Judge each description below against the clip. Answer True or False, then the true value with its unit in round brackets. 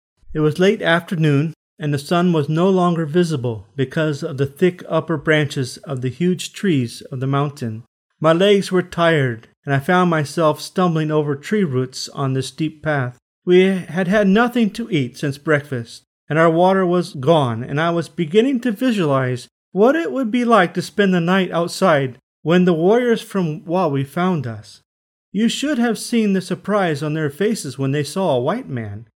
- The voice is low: False (165 Hz)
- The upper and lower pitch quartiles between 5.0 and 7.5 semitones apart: True (5.3 semitones)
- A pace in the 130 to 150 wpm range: False (185 wpm)